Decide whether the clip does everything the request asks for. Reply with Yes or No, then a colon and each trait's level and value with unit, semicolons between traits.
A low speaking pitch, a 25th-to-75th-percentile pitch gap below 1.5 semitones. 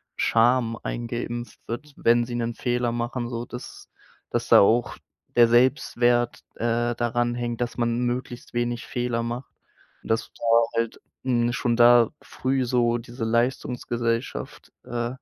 Yes: low, 120 Hz; narrow, 0.7 semitones